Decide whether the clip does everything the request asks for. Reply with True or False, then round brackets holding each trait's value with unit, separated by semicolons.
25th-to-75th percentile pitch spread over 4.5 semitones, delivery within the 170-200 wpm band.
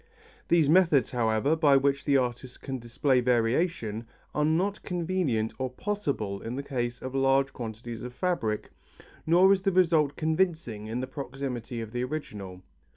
False (5.1 semitones; 155 wpm)